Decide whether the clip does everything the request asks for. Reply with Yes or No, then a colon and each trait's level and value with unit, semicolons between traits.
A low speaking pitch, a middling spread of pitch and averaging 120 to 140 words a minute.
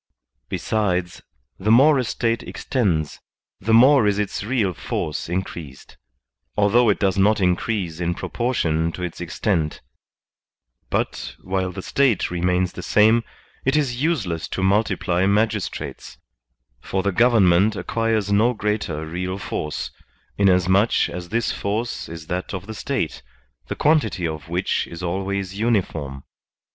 Yes: low, 100 Hz; average, 4.1 semitones; slow, 135 wpm